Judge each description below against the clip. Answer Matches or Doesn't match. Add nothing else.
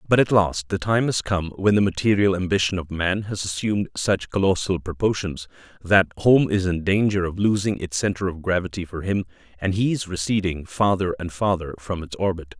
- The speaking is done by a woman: Doesn't match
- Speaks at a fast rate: Doesn't match